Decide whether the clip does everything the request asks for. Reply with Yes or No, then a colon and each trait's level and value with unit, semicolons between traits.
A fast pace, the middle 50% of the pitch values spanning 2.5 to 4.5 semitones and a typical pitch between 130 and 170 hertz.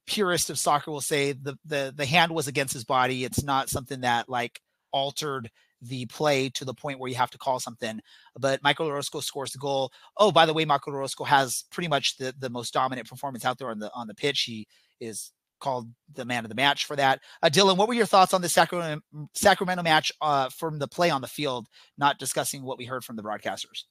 Yes: fast, 235 wpm; average, 3.0 semitones; medium, 140 Hz